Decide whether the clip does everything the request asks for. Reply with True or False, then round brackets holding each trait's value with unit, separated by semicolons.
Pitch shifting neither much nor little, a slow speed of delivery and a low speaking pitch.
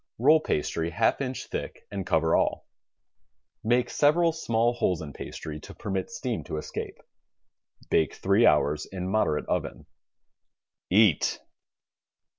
False (7.1 semitones; 125 wpm; 100 Hz)